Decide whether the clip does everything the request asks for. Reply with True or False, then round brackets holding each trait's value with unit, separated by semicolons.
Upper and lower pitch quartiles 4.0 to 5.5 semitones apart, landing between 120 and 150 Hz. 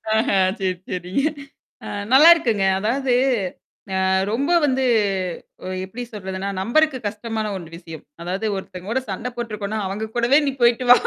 False (5.0 semitones; 220 Hz)